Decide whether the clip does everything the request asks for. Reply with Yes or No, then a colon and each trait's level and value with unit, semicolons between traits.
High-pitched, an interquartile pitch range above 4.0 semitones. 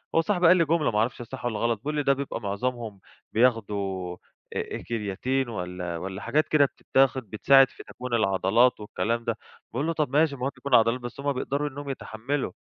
No: low, 125 Hz; average, 4.6 semitones